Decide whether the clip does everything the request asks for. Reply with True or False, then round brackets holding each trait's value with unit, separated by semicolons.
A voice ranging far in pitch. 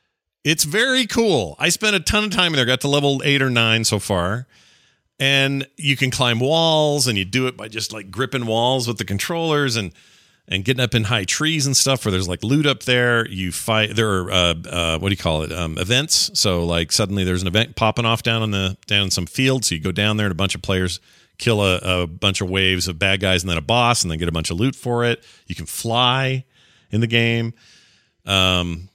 True (5.9 semitones)